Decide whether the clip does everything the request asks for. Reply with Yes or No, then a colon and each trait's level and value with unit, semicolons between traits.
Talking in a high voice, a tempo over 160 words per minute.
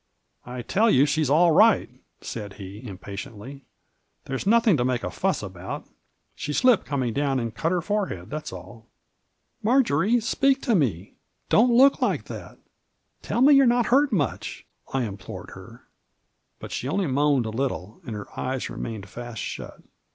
No: medium, 140 Hz; average, 175 wpm